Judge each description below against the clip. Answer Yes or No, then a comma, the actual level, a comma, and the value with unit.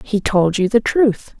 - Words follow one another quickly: Yes, fast, 215 wpm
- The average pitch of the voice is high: Yes, high, 215 Hz